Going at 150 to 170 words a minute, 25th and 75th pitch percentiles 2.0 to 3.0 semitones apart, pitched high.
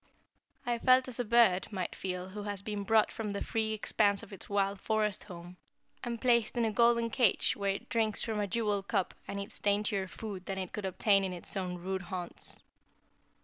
No: fast, 205 wpm; narrow, 2.6 semitones; high, 205 Hz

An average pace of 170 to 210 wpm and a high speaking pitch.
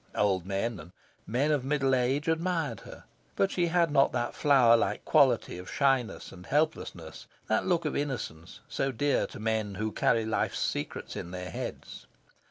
No: average, 175 wpm; low, 125 Hz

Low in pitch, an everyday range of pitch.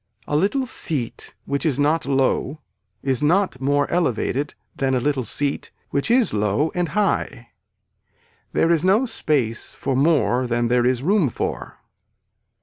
No: medium, 145 Hz; average, 4.7 semitones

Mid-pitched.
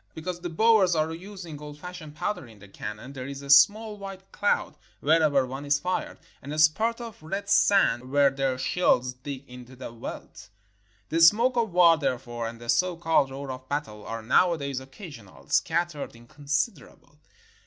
Yes: medium, 150 Hz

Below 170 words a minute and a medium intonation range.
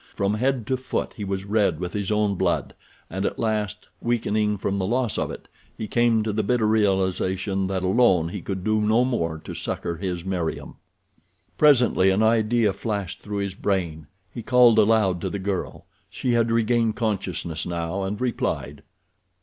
No: average, 175 wpm; average, 3.1 semitones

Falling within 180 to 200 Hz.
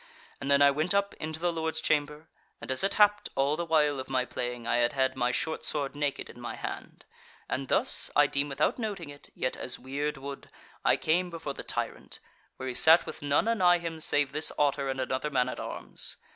No: medium, 145 Hz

